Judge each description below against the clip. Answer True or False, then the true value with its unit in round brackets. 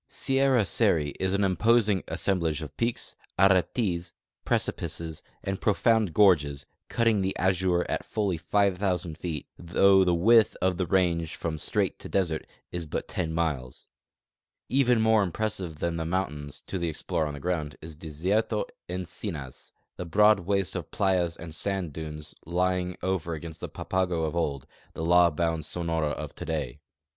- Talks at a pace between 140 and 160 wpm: True (155 wpm)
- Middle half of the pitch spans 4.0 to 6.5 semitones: False (3.2 semitones)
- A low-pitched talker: True (90 Hz)